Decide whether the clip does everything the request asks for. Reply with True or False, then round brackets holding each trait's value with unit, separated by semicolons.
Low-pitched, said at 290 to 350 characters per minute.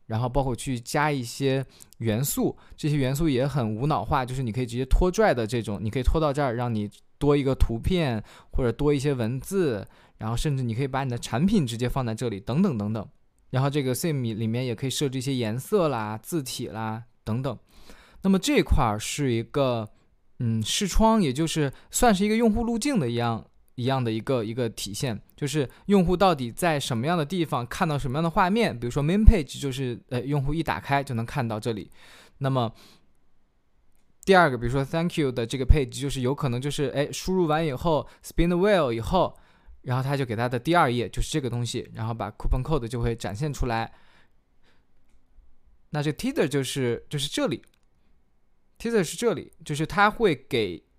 True (130 Hz; 340 characters per minute)